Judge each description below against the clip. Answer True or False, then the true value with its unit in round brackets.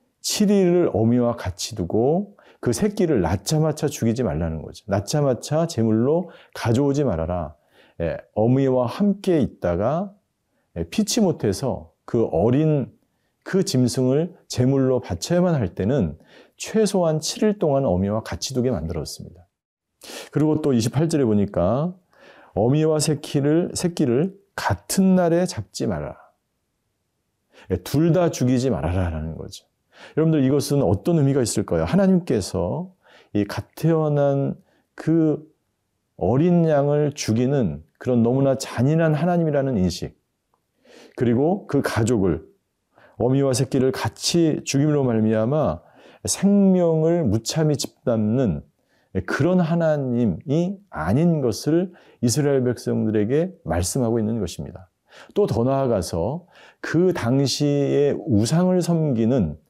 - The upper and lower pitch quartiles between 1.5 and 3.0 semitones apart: False (6.4 semitones)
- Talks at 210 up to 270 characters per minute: True (255 characters per minute)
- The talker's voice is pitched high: False (140 Hz)